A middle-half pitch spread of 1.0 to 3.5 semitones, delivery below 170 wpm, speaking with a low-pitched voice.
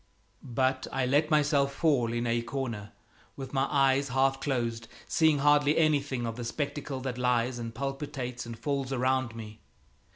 Yes: average, 2.9 semitones; average, 160 wpm; low, 130 Hz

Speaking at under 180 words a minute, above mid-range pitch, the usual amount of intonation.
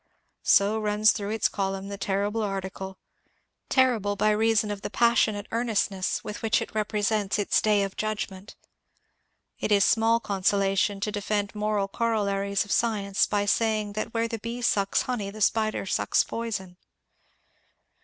No: average, 155 wpm; high, 210 Hz; narrow, 1.8 semitones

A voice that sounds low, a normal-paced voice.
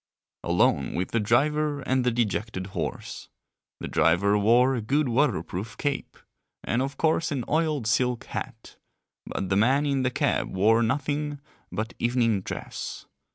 Yes: low, 120 Hz; average, 150 wpm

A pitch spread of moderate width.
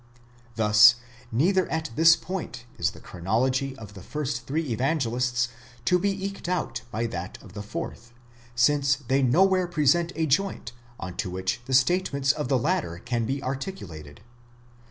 No: wide, 6.1 semitones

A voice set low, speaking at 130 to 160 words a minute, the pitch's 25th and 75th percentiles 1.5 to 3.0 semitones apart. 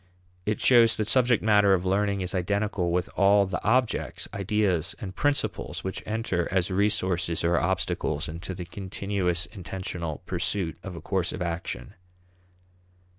Yes: very low, 95 Hz; average, 145 wpm; average, 2.7 semitones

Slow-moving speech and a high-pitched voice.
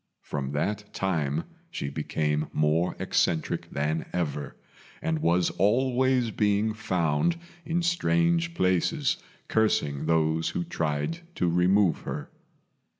No: slow, 110 wpm; very low, 90 Hz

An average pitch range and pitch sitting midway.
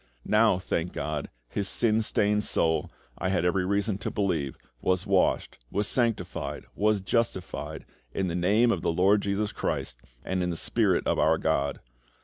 No: average, 3.4 semitones; very low, 95 Hz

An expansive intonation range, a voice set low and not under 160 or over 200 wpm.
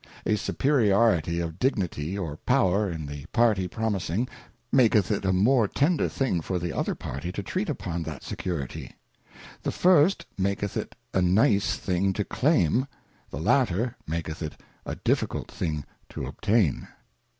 No: wide, 5.7 semitones; very low, 95 Hz; average, 150 wpm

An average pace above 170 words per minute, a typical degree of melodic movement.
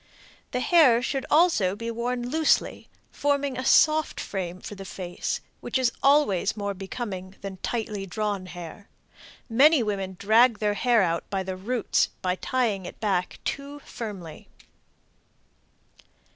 No: slow, 135 wpm; average, 4.9 semitones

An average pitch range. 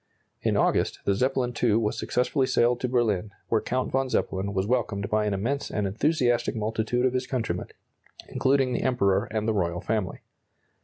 Yes: average, 3.6 semitones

